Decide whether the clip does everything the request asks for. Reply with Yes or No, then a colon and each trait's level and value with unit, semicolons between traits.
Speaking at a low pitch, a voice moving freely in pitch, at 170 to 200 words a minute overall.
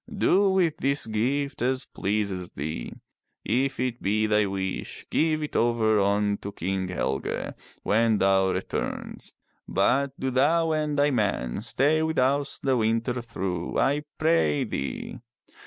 No: low, 120 Hz; wide, 6.0 semitones; average, 140 wpm